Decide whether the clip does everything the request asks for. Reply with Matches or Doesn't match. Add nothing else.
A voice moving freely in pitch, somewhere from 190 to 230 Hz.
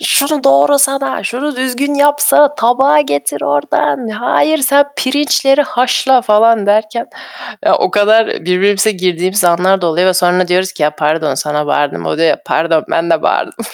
Matches